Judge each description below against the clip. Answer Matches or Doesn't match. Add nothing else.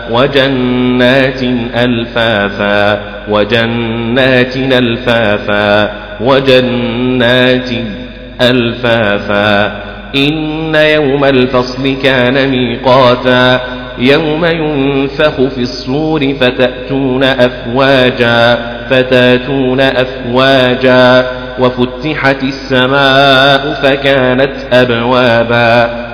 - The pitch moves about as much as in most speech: Doesn't match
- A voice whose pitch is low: Matches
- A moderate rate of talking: Doesn't match